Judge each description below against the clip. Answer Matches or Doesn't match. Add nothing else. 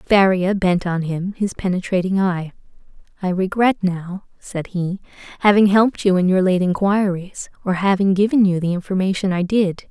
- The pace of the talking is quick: Doesn't match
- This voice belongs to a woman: Matches